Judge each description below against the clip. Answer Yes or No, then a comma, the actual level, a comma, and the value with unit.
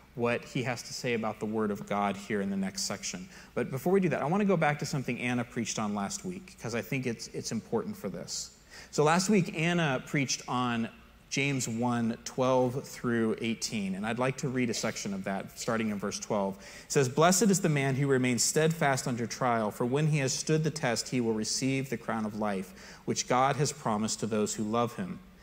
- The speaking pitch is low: Yes, low, 130 Hz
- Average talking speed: No, fast, 230 wpm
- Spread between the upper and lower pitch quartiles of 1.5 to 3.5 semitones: No, wide, 5.4 semitones